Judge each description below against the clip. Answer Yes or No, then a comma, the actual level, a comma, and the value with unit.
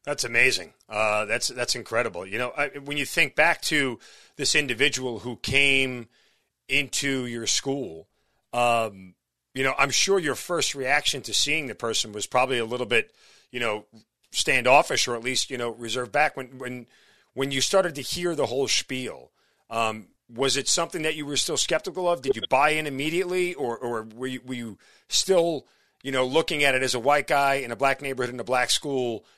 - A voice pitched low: Yes, low, 130 Hz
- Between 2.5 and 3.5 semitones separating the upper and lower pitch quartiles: Yes, average, 3.2 semitones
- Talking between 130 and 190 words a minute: No, average, 200 wpm